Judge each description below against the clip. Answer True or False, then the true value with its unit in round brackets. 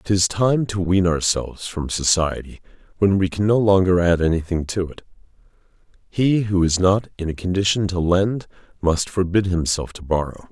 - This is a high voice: False (90 Hz)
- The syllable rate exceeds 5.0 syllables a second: False (4.9 syllables/s)